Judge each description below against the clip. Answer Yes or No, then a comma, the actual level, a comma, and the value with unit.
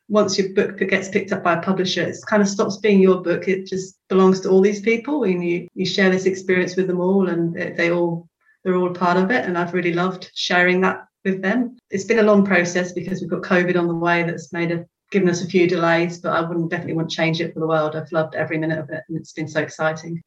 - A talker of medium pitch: Yes, medium, 180 Hz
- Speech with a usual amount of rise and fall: No, narrow, 2.0 semitones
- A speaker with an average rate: No, fast, 265 wpm